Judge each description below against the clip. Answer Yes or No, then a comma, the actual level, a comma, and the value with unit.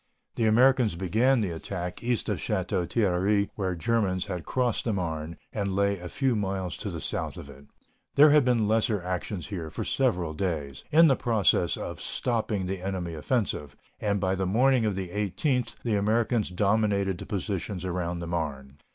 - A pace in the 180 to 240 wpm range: Yes, average, 185 wpm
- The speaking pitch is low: Yes, low, 100 Hz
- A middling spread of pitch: Yes, average, 4.2 semitones